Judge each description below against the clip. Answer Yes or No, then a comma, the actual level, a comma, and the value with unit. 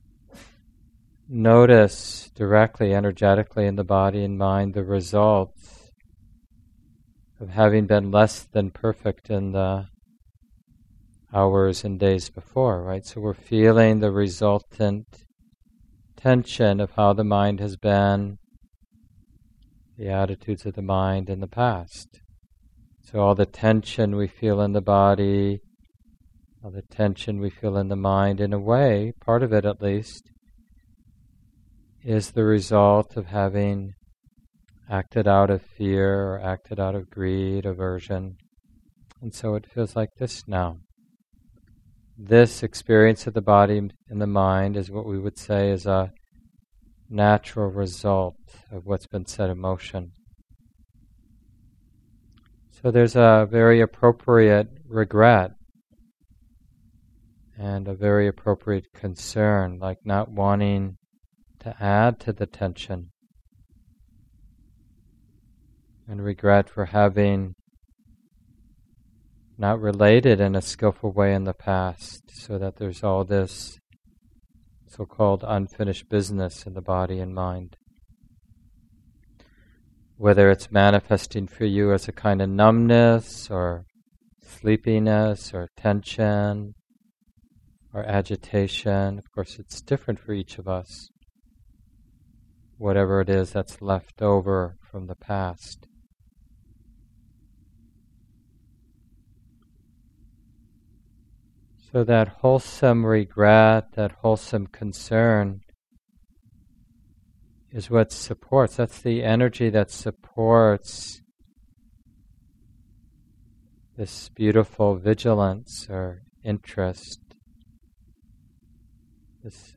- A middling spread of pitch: No, narrow, 2.3 semitones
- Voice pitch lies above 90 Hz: Yes, low, 105 Hz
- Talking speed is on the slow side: Yes, slow, 105 wpm